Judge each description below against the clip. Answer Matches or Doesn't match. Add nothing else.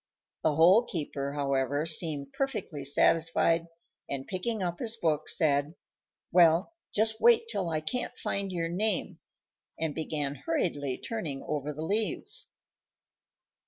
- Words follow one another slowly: Matches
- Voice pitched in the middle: Matches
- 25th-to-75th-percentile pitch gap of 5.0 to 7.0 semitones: Matches